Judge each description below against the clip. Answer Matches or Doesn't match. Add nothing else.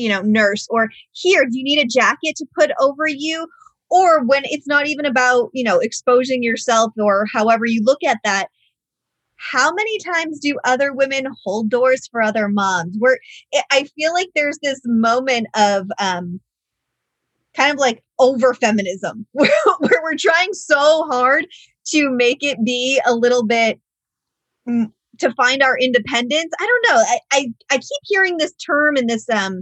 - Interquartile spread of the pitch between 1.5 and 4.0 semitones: Doesn't match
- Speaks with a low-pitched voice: Doesn't match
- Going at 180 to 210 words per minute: Doesn't match